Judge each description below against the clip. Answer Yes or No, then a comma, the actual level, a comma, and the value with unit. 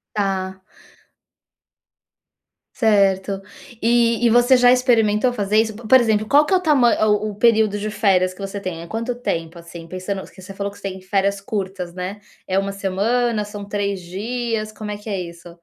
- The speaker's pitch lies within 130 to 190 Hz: No, high, 205 Hz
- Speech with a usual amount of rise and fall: Yes, average, 3.0 semitones